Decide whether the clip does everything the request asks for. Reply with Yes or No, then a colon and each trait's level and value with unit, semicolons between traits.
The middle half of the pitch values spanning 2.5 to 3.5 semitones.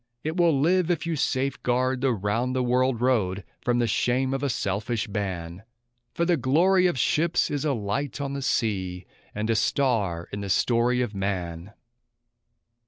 No: average, 5.3 semitones